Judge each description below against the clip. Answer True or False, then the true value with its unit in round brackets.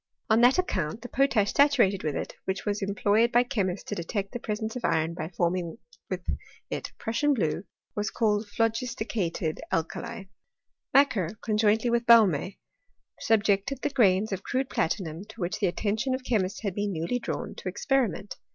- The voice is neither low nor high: False (210 Hz)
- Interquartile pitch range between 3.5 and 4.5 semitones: True (4.0 semitones)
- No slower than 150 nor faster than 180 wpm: True (170 wpm)